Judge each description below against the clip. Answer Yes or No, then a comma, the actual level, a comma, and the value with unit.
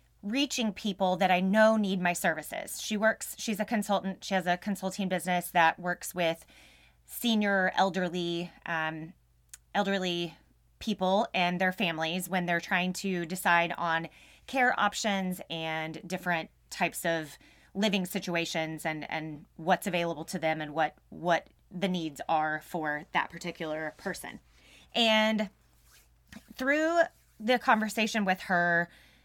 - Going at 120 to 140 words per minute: Yes, slow, 135 wpm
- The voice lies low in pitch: No, medium, 180 Hz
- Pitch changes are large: No, average, 3.8 semitones